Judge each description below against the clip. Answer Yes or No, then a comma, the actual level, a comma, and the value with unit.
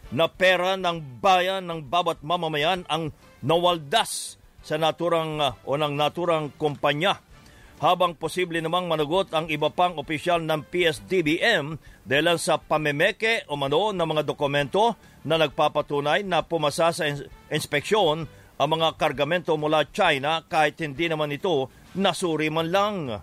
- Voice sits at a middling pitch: Yes, medium, 160 Hz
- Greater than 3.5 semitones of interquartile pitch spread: No, average, 2.8 semitones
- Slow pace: Yes, slow, 130 wpm